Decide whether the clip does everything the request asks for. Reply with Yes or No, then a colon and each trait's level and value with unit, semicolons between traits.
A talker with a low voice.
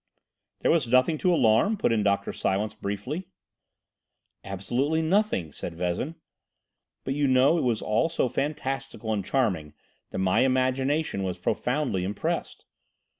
Yes: low, 125 Hz